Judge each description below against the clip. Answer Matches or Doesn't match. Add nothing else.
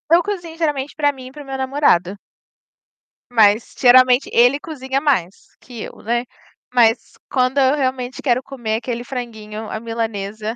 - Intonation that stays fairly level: Doesn't match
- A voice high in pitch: Matches